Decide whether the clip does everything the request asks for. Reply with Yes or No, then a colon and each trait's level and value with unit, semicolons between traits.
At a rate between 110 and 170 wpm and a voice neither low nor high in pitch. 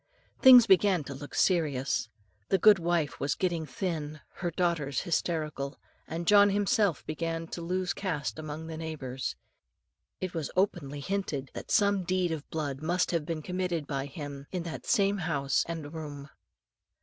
Yes: average, 155 wpm; medium, 165 Hz